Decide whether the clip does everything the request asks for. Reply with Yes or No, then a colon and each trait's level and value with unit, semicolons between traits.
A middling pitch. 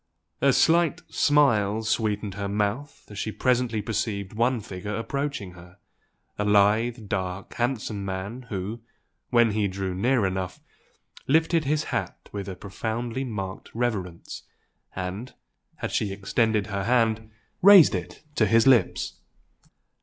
No: low, 110 Hz